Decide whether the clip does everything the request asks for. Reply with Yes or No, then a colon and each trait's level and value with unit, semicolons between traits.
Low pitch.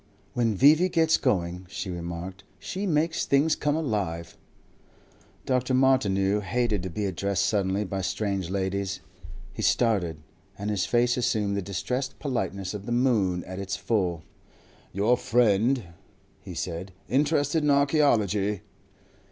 Yes: low, 105 Hz